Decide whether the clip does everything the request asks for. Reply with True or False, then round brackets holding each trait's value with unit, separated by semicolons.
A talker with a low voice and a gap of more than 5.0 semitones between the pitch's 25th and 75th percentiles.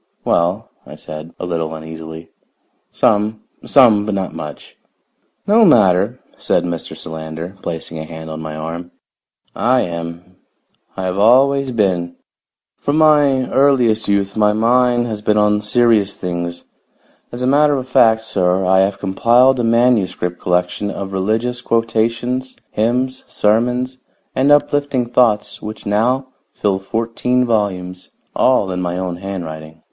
True (105 Hz; 5.6 semitones)